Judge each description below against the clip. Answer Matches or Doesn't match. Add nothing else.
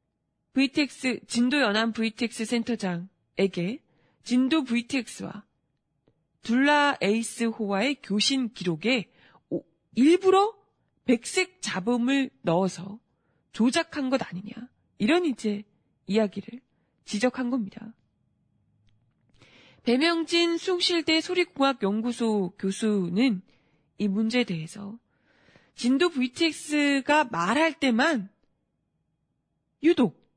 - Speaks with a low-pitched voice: Doesn't match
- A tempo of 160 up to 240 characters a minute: Matches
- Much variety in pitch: Matches